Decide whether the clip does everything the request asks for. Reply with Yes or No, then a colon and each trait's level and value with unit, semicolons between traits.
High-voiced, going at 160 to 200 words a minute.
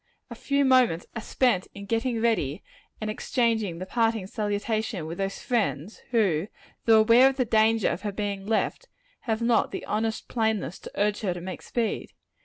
Yes: high, 220 Hz; average, 185 wpm